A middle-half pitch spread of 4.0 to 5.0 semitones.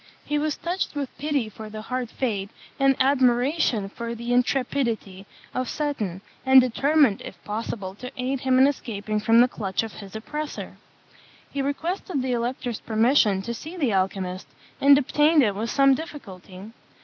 Yes: average, 4.6 semitones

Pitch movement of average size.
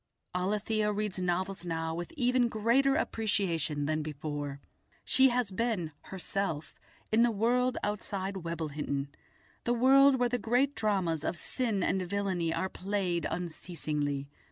No: wide, 5.8 semitones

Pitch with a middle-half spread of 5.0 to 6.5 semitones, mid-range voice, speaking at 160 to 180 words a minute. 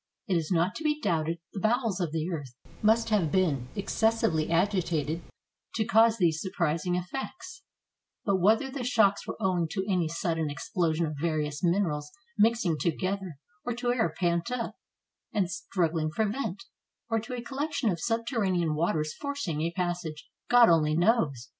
Yes: wide, 5.5 semitones; medium, 180 Hz; average, 165 wpm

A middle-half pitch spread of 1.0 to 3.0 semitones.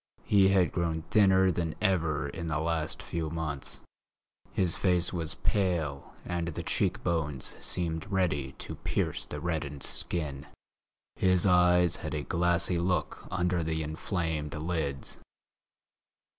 Yes: narrow, 2.5 semitones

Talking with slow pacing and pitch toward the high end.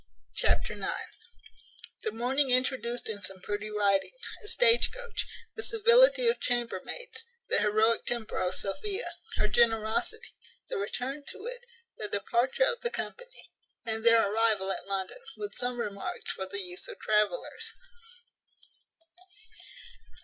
Yes: slow, 130 wpm; high, 235 Hz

